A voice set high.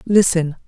No: medium, 175 Hz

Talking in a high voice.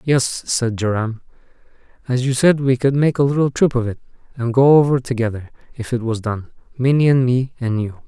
No: low, 125 Hz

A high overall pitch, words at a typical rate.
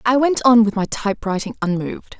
Yes: high, 220 Hz; average, 190 wpm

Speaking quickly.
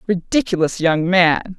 No: slow, 115 wpm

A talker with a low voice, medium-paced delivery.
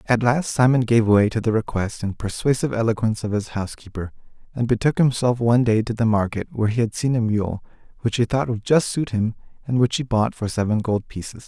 No: low, 115 Hz; fast, 225 wpm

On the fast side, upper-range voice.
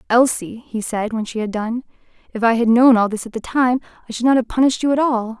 Yes: fast, 265 wpm; high, 235 Hz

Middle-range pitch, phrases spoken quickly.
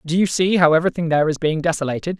Yes: medium, 165 Hz; fast, 245 wpm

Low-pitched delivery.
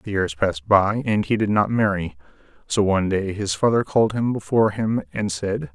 Yes: low, 100 Hz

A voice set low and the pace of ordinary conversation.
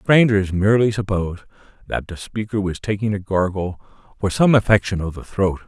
Yes: low, 100 Hz; average, 170 wpm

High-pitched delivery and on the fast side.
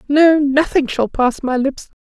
No: very high, 280 Hz; average, 175 wpm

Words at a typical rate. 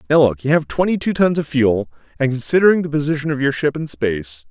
No: fast, 215 wpm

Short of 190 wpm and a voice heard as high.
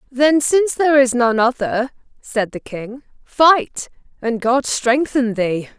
Yes: average, 145 wpm; very high, 250 Hz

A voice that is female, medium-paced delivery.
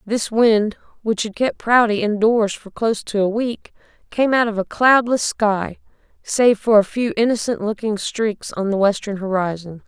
Yes: female; average, 175 wpm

